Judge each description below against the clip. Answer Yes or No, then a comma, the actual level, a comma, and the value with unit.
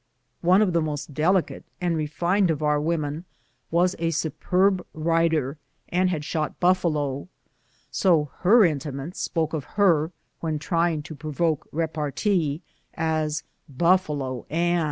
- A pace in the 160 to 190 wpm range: No, slow, 135 wpm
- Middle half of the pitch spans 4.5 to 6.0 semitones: No, average, 2.7 semitones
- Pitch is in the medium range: Yes, medium, 160 Hz